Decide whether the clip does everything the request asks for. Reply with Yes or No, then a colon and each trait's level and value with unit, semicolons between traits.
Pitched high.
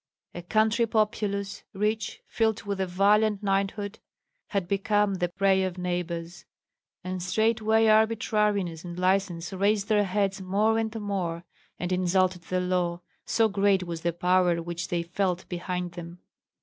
Yes: high, 195 Hz